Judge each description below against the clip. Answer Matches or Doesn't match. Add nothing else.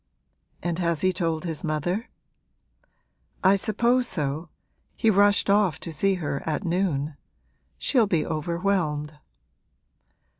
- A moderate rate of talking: Doesn't match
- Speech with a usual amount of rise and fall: Matches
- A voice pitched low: Doesn't match